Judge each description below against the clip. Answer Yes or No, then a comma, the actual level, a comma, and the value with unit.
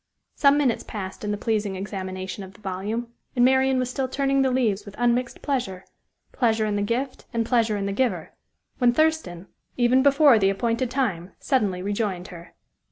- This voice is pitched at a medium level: No, high, 230 Hz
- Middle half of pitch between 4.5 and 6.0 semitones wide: Yes, average, 4.8 semitones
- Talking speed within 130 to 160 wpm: No, average, 180 wpm